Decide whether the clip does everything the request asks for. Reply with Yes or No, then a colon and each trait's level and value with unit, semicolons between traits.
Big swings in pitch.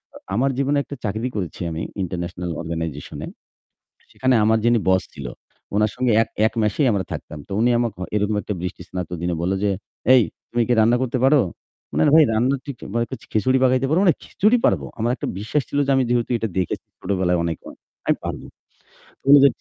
Yes: wide, 5.9 semitones